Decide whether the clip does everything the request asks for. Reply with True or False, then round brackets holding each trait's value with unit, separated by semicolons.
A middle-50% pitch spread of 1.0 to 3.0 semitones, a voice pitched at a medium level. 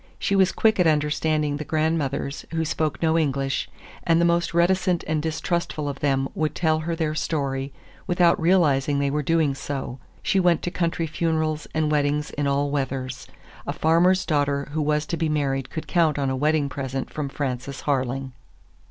True (2.7 semitones; 150 Hz)